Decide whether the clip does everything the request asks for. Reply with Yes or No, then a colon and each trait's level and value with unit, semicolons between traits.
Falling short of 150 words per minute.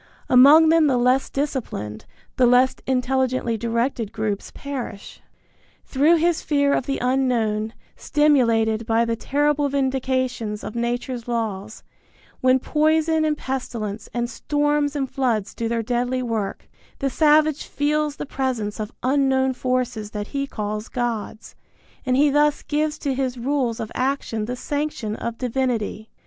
Yes: average, 140 wpm